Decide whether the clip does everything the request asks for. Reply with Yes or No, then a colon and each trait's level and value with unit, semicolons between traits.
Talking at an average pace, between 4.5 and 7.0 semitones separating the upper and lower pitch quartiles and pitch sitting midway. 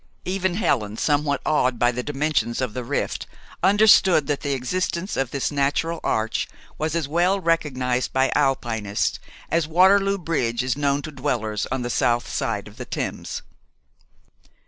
Yes: average, 155 wpm; average, 5.1 semitones; medium, 145 Hz